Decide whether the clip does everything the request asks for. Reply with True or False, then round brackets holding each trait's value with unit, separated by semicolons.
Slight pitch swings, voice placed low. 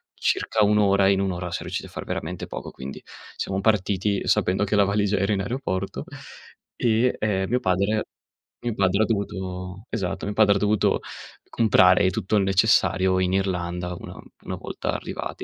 True (2.2 semitones; 100 Hz)